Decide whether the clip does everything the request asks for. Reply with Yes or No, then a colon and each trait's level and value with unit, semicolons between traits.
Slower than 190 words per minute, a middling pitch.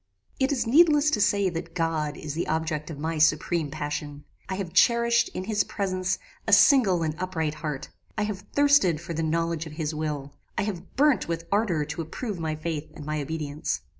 No: average, 195 wpm; medium, 165 Hz